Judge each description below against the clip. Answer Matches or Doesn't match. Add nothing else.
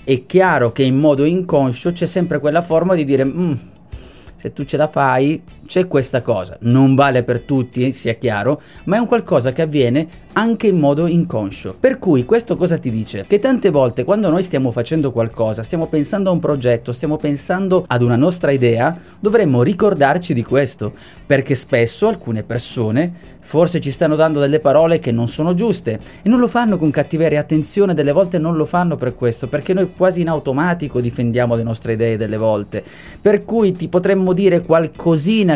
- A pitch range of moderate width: Doesn't match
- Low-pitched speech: Doesn't match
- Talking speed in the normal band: Doesn't match